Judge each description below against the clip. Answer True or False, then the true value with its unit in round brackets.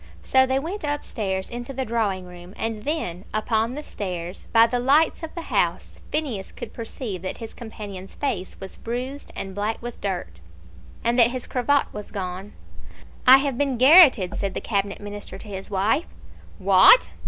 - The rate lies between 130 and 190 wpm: True (175 wpm)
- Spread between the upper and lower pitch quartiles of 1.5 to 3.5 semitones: False (5.3 semitones)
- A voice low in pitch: False (225 Hz)